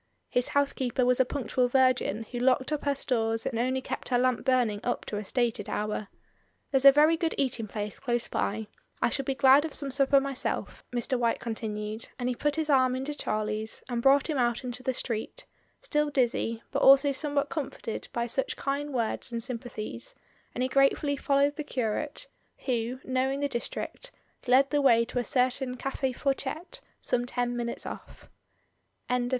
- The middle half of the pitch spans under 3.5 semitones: Yes, average, 2.7 semitones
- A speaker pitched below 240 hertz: No, very high, 255 Hz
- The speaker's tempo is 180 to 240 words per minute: Yes, average, 185 wpm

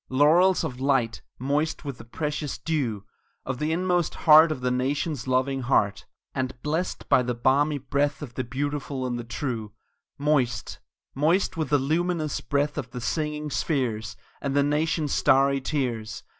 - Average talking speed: Yes, average, 160 wpm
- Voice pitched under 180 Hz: Yes, medium, 140 Hz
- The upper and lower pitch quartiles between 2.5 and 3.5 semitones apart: Yes, average, 3.1 semitones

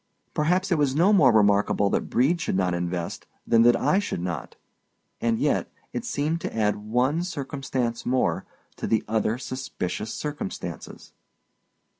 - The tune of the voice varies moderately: No, wide, 6.3 semitones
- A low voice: Yes, low, 125 Hz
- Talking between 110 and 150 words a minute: Yes, average, 145 wpm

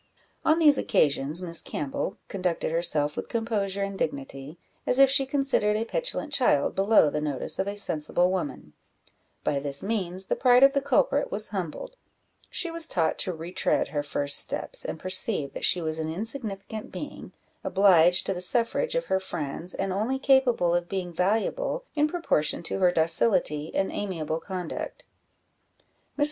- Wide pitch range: Yes, wide, 6.4 semitones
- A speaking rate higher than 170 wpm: No, average, 165 wpm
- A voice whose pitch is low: No, high, 190 Hz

